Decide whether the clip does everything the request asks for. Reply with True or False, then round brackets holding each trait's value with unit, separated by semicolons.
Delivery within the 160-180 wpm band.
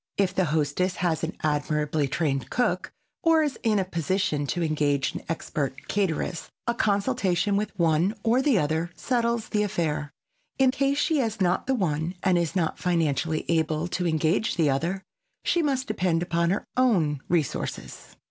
True (165 wpm)